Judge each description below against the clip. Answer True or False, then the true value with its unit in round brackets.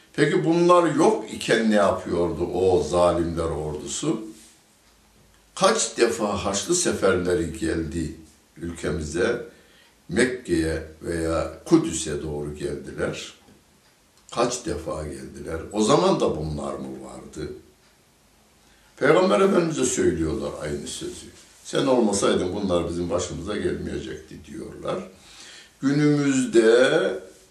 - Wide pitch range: True (6.2 semitones)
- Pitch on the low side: True (85 Hz)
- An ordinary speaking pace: False (90 wpm)